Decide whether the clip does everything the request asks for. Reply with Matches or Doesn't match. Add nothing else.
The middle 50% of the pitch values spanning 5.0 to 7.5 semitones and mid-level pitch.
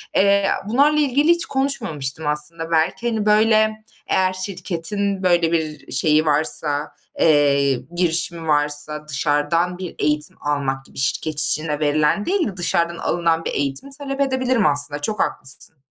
Matches